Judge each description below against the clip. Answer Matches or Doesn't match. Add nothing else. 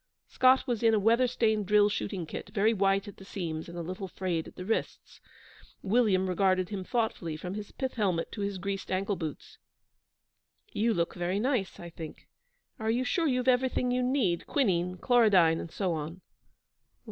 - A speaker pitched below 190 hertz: Doesn't match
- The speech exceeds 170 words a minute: Matches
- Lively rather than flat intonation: Doesn't match